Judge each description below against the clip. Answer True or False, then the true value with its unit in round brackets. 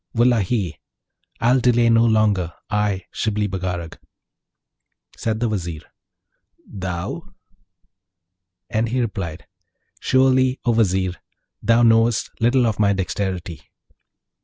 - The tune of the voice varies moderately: True (3.8 semitones)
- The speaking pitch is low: True (110 Hz)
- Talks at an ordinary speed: False (100 wpm)